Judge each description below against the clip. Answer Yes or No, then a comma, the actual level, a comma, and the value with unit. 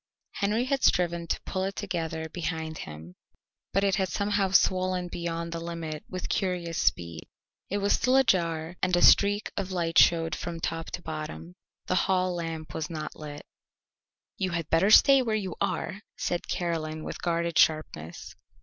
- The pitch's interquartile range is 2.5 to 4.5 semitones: Yes, average, 2.9 semitones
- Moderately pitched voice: Yes, medium, 170 Hz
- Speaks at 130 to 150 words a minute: No, average, 165 wpm